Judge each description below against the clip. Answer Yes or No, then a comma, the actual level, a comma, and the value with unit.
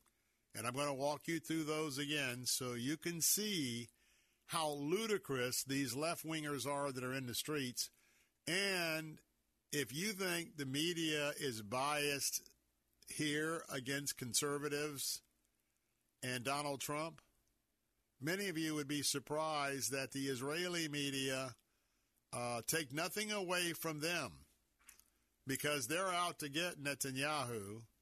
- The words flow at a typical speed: No, slow, 130 wpm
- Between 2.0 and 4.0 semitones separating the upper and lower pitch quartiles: Yes, average, 3.1 semitones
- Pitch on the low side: No, medium, 145 Hz